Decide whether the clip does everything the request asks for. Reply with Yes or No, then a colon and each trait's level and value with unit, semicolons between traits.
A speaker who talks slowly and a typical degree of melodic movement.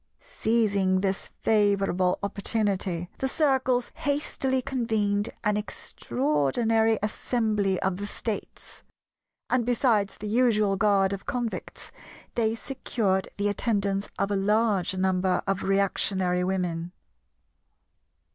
Yes: slow, 105 wpm; average, 3.0 semitones